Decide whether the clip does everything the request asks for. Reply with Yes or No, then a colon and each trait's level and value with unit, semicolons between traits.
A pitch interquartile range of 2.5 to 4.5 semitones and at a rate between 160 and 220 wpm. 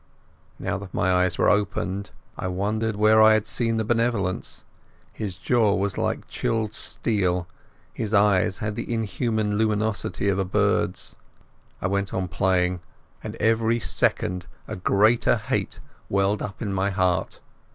No: average, 2.8 semitones; average, 150 wpm